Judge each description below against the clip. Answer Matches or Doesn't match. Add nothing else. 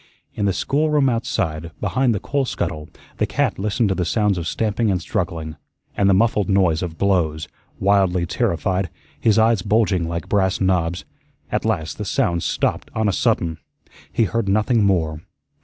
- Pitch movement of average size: Matches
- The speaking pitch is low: Matches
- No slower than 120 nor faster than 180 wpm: Matches